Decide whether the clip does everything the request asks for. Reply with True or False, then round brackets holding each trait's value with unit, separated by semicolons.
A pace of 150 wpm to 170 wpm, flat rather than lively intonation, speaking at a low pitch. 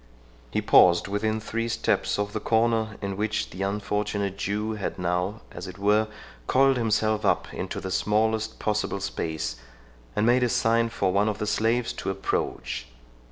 True (165 wpm; 2.1 semitones; 105 Hz)